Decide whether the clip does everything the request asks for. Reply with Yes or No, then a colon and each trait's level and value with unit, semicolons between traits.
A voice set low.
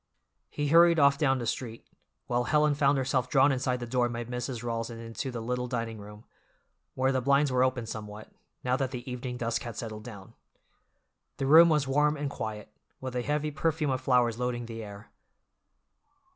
Yes: low, 125 Hz